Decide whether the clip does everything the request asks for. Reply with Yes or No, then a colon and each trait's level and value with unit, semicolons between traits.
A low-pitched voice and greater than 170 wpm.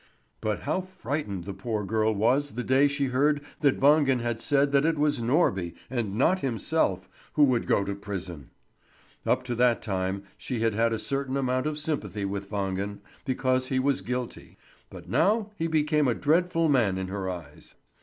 Yes: low, 125 Hz; average, 185 wpm